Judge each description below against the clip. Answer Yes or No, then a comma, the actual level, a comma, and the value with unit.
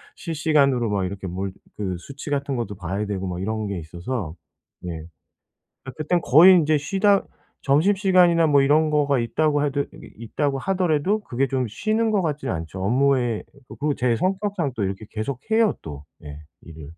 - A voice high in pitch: No, low, 135 Hz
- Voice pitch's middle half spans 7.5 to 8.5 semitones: Yes, wide, 7.8 semitones